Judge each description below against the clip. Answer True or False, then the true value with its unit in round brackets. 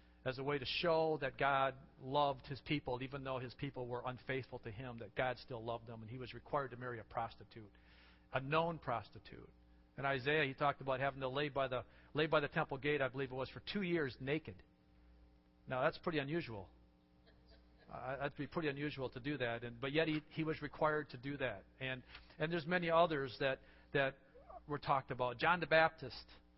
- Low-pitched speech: True (130 Hz)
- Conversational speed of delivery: False (210 wpm)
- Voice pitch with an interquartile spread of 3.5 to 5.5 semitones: True (4.0 semitones)